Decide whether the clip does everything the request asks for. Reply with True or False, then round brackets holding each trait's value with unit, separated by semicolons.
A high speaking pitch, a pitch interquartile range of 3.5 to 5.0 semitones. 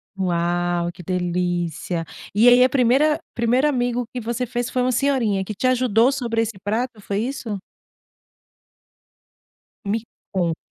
False (225 Hz; 5.4 semitones)